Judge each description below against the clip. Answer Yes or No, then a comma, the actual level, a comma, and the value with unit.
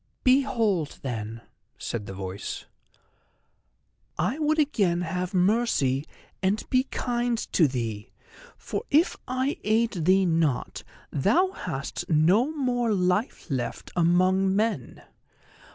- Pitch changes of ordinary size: No, wide, 7.9 semitones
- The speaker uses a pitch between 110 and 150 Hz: No, high, 190 Hz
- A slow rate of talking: Yes, slow, 110 wpm